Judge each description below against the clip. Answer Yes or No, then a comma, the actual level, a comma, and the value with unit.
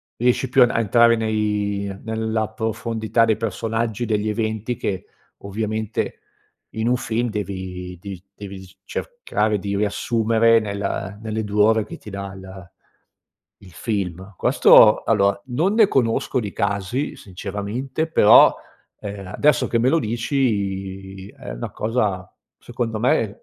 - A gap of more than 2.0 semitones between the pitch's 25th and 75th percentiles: Yes, narrow, 2.5 semitones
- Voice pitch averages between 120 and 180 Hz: No, low, 110 Hz